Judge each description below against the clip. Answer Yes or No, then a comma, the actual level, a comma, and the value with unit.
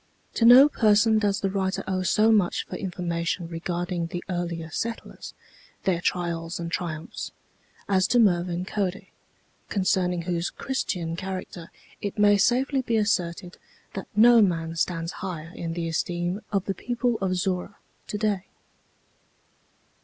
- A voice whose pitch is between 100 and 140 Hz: No, medium, 185 Hz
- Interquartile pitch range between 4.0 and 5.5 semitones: No, average, 3.2 semitones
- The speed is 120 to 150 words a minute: Yes, average, 140 wpm